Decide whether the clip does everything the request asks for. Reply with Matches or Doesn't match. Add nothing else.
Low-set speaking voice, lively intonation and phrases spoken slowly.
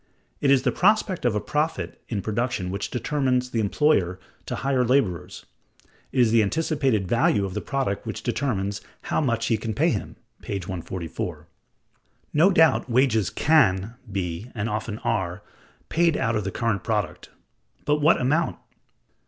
Doesn't match